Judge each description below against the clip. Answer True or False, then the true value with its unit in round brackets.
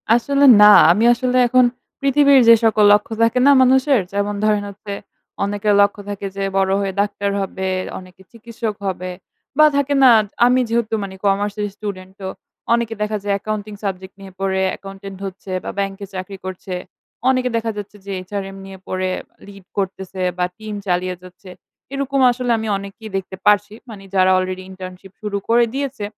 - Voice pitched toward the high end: True (205 Hz)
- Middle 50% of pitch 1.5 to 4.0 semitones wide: True (3.2 semitones)